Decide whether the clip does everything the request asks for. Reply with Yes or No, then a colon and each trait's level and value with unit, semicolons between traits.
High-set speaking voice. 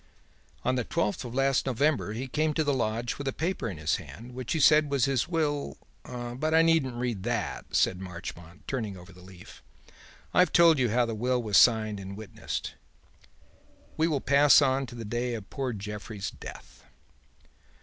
No: low, 125 Hz